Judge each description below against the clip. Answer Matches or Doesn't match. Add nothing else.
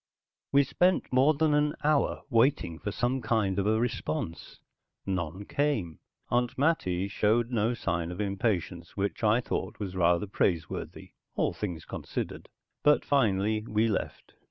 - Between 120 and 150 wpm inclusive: Matches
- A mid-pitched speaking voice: Doesn't match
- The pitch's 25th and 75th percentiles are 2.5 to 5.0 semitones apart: Doesn't match